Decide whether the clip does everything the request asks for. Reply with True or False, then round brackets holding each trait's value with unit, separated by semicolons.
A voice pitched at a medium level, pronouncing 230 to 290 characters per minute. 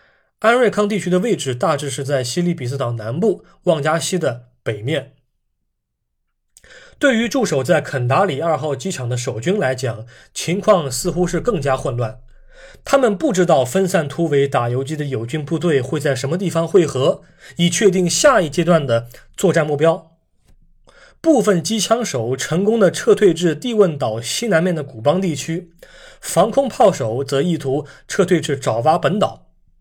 True (165 Hz; 250 characters per minute)